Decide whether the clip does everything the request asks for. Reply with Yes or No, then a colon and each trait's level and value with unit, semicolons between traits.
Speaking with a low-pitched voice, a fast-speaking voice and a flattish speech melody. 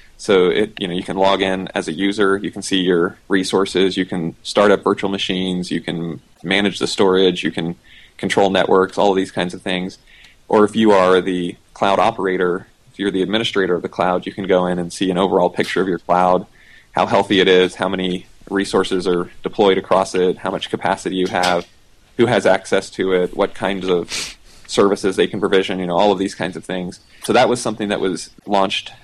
Yes: very low, 95 Hz; fast, 220 wpm; narrow, 1.4 semitones